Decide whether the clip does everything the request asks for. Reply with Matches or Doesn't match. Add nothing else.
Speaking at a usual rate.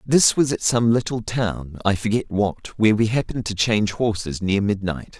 Matches